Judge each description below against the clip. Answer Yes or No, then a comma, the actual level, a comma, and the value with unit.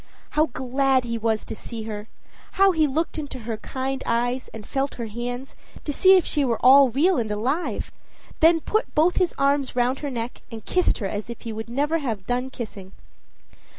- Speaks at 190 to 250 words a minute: Yes, average, 200 wpm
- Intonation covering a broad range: No, average, 4.2 semitones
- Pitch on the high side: Yes, very high, 255 Hz